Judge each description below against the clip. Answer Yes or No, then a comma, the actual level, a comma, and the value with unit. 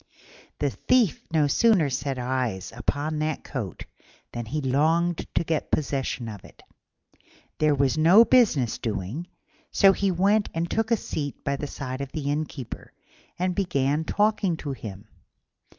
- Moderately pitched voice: Yes, medium, 150 Hz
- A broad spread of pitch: No, average, 4.9 semitones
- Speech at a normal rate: Yes, average, 150 wpm